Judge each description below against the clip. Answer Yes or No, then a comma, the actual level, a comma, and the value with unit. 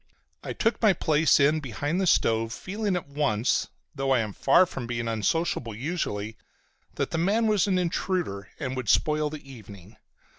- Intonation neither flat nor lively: No, wide, 7.4 semitones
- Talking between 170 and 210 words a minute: Yes, average, 175 wpm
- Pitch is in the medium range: Yes, medium, 145 Hz